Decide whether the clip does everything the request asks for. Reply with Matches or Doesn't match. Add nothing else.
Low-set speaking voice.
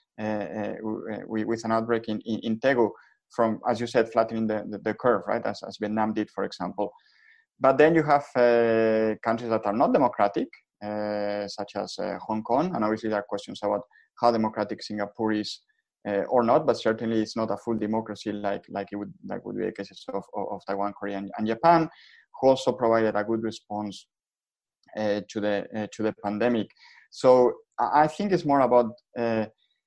Matches